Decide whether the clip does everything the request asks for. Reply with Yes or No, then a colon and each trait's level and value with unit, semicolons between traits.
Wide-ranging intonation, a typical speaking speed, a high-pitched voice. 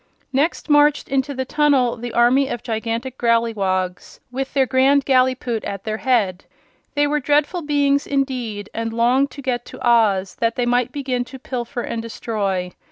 No: average, 3.2 semitones; average, 165 wpm; very high, 250 Hz